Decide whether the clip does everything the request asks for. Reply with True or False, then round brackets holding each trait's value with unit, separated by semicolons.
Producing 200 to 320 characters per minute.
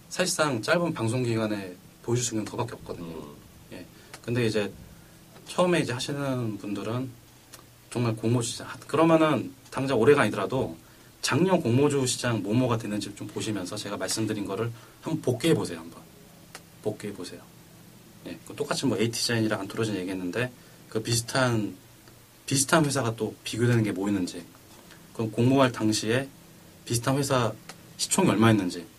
False (335 characters per minute)